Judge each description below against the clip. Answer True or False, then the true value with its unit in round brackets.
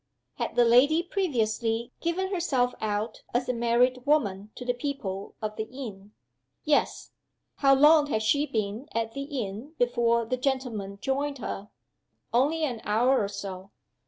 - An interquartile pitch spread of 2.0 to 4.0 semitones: False (4.4 semitones)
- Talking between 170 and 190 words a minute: False (155 wpm)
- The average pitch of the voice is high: True (245 Hz)